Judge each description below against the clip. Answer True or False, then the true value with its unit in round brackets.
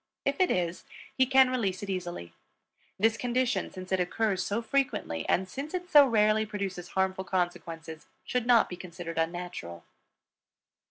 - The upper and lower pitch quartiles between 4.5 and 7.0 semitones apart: True (5.5 semitones)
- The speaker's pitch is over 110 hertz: True (190 Hz)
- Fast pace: False (155 wpm)